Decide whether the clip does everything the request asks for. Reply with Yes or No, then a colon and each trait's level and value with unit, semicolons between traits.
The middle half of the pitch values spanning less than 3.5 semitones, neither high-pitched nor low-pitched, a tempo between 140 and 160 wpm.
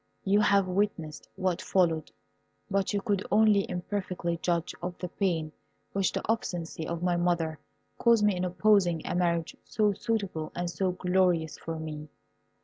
Yes: average, 2.9 semitones; medium, 180 Hz; average, 155 wpm